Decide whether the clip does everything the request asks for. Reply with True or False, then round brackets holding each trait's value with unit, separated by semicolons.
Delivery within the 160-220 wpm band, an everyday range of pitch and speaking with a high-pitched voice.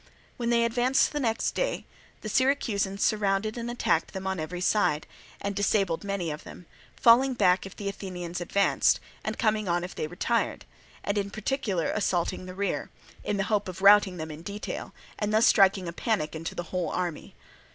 True (185 wpm; 3.3 semitones; 200 Hz)